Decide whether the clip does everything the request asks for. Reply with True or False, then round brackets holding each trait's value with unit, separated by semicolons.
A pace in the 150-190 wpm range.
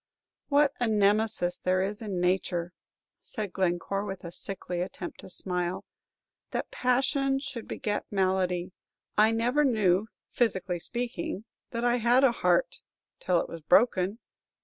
False (140 wpm)